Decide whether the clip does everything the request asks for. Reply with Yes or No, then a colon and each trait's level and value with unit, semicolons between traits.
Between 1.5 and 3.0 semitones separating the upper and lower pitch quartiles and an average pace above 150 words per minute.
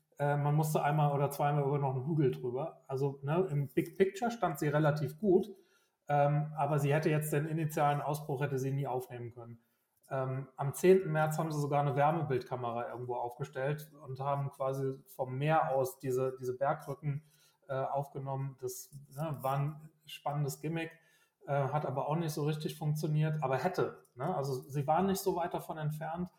Yes: narrow, 2.6 semitones; average, 180 wpm